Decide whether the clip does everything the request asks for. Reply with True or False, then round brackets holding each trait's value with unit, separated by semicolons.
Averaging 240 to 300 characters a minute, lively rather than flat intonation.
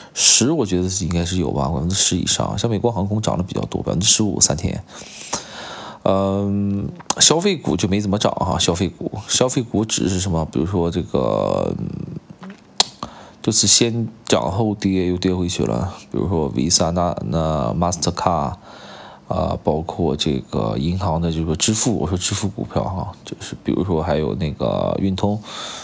False (275 characters per minute; 4.0 semitones)